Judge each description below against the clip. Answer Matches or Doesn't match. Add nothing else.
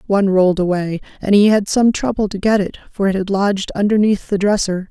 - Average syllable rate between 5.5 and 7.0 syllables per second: Matches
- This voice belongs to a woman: Matches